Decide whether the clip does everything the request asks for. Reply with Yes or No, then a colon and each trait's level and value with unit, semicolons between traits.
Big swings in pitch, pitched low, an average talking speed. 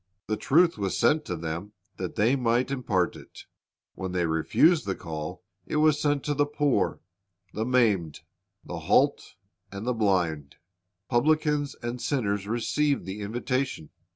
Yes: wide, 7.0 semitones; low, 115 Hz; average, 150 wpm